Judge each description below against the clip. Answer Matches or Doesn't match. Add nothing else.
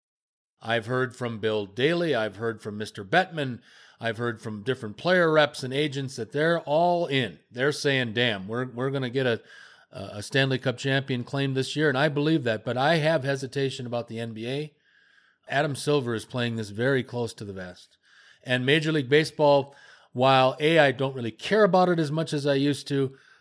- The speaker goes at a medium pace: Matches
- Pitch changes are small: Doesn't match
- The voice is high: Doesn't match